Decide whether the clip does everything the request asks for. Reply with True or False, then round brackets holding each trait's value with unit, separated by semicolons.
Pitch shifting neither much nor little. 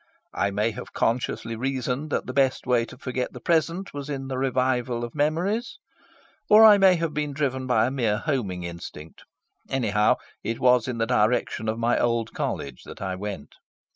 True (3.8 semitones)